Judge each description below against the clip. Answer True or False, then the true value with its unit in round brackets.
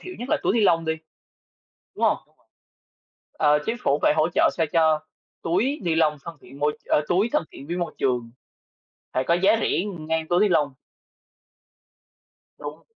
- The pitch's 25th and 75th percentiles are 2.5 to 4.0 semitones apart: True (3.5 semitones)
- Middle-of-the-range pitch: True (165 Hz)